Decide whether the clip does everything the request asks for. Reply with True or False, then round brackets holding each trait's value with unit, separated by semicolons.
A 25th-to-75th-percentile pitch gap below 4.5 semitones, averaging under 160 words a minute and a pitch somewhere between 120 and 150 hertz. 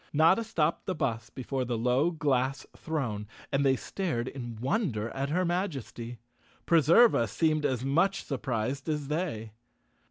False (5.2 semitones; 140 wpm; 135 Hz)